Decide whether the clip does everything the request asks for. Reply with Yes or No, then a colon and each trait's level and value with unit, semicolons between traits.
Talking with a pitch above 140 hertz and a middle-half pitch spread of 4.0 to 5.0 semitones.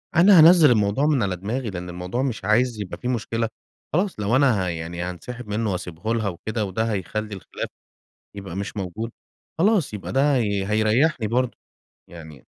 No: low, 110 Hz; average, 4.7 semitones